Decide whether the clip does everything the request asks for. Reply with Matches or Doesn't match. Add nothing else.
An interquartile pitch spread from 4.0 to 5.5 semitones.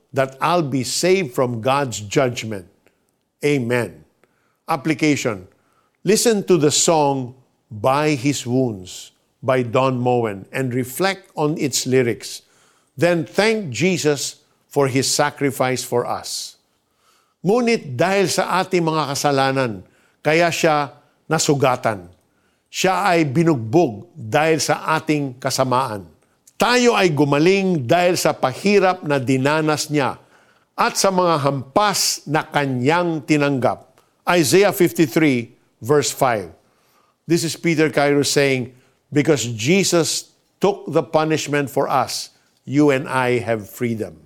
Matches